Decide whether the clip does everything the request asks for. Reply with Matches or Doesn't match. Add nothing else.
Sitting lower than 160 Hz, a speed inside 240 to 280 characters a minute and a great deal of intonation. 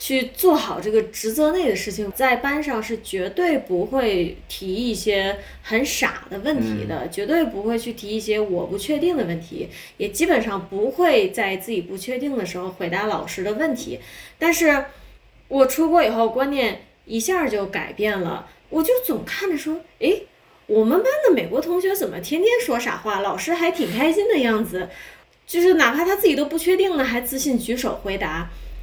Doesn't match